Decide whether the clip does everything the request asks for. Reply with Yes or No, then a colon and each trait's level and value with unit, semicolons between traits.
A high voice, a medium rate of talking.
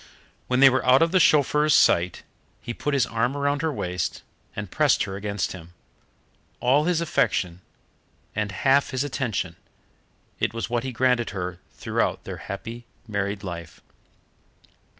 No: low, 120 Hz; average, 150 wpm